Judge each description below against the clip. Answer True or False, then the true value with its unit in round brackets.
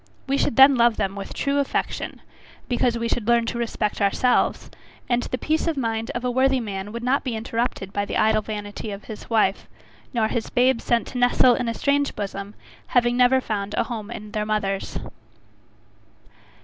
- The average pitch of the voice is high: True (235 Hz)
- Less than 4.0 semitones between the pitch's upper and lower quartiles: True (2.9 semitones)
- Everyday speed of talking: True (190 wpm)